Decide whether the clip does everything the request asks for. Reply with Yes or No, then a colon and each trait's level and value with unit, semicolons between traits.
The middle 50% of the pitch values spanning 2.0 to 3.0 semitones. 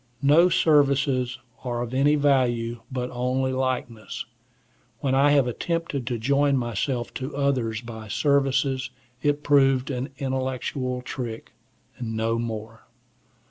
Yes: average, 2.7 semitones